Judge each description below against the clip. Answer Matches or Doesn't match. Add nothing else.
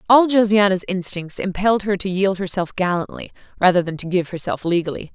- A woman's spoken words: Matches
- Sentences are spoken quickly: Doesn't match